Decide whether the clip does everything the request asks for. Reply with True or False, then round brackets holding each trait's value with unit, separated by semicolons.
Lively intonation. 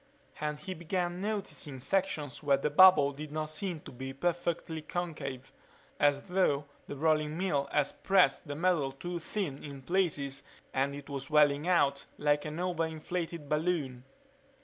False (3.8 semitones)